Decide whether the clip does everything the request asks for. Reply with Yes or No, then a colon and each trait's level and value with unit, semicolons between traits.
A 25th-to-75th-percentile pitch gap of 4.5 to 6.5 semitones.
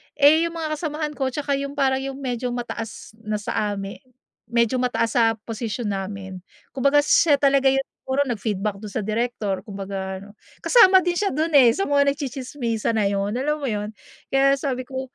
Yes: average, 4.9 semitones